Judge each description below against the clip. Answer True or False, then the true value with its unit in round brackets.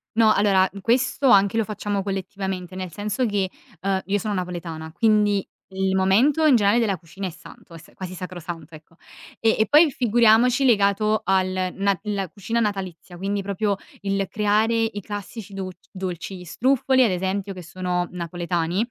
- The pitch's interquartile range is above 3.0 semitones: False (2.7 semitones)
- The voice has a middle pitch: False (195 Hz)